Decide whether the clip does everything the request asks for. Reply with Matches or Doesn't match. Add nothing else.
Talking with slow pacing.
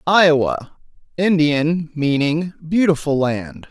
Matches